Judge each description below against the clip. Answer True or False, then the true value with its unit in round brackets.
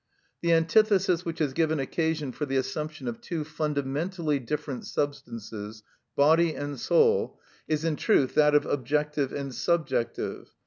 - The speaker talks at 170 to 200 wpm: False (140 wpm)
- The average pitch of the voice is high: False (150 Hz)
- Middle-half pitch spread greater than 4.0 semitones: False (3.0 semitones)